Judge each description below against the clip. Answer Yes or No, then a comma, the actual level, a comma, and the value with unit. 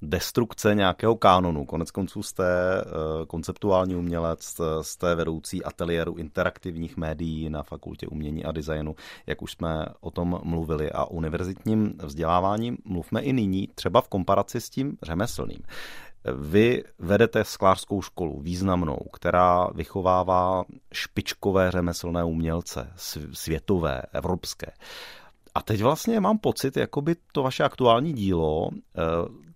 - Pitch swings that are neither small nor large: Yes, average, 3.6 semitones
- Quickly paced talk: No, average, 120 wpm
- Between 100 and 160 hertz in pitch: No, very low, 90 Hz